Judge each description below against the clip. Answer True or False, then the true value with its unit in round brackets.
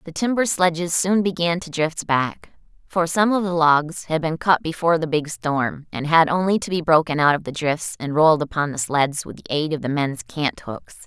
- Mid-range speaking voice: True (160 Hz)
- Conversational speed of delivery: False (230 wpm)